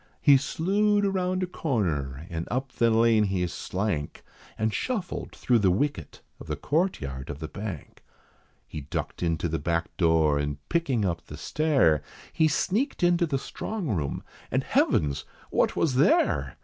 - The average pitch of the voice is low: Yes, low, 110 Hz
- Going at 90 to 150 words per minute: No, average, 160 wpm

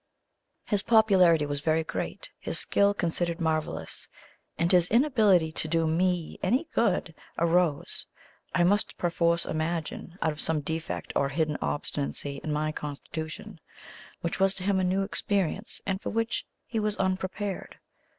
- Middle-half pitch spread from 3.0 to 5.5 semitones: Yes, average, 3.6 semitones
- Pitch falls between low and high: Yes, medium, 170 Hz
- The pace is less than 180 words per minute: Yes, average, 150 wpm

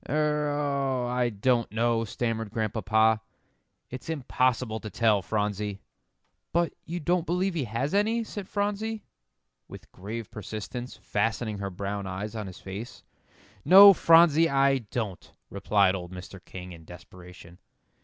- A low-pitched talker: Yes, low, 115 Hz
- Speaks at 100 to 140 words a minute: Yes, slow, 135 wpm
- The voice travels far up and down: Yes, wide, 6.5 semitones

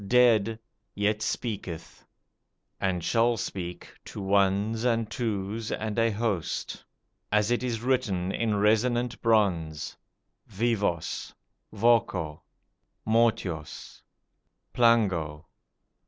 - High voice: No, low, 105 Hz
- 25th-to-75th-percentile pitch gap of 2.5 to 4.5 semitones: Yes, average, 3.3 semitones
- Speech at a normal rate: No, slow, 90 wpm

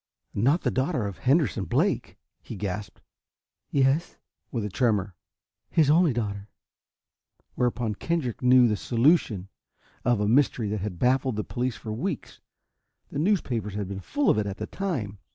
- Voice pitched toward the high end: No, low, 120 Hz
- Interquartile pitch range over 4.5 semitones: Yes, average, 5.0 semitones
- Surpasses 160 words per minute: No, average, 155 wpm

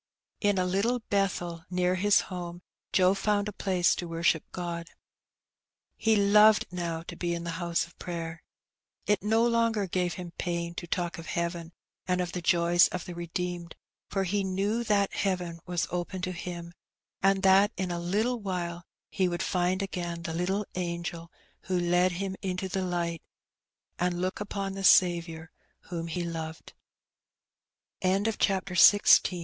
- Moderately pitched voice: Yes, medium, 180 Hz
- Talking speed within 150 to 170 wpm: Yes, average, 165 wpm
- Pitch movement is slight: Yes, narrow, 2.2 semitones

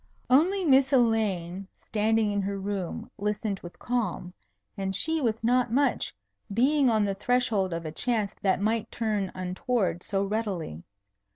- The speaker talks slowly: No, average, 150 wpm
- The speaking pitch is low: No, high, 210 Hz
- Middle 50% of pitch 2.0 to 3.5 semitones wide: No, average, 4.0 semitones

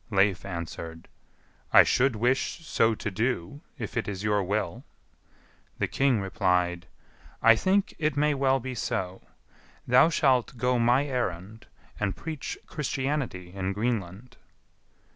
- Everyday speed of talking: No, slow, 130 wpm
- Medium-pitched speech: No, low, 115 Hz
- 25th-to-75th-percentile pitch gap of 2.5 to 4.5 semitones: No, wide, 5.6 semitones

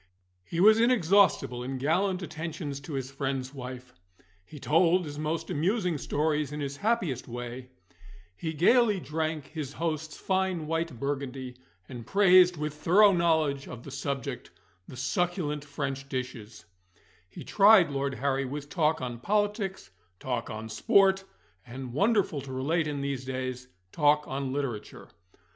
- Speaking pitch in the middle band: Yes, medium, 150 Hz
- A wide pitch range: No, average, 4.7 semitones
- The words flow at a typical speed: Yes, average, 145 wpm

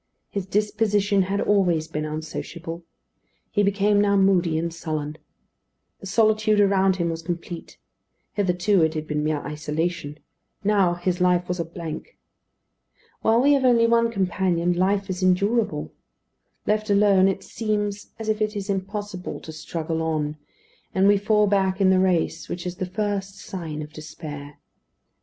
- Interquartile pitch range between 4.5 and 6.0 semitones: No, average, 3.7 semitones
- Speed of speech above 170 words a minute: No, average, 155 wpm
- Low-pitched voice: No, high, 190 Hz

